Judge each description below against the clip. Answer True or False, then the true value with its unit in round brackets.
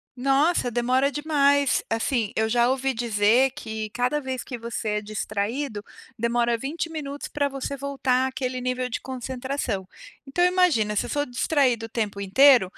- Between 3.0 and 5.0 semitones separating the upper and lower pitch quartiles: True (3.7 semitones)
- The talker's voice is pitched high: True (255 Hz)